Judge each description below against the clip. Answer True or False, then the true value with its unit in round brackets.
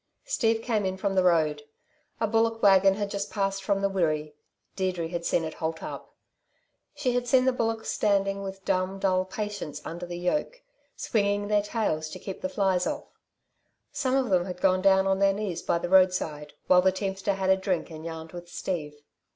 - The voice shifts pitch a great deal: False (2.8 semitones)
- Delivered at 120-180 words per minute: False (200 wpm)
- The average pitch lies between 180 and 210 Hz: True (190 Hz)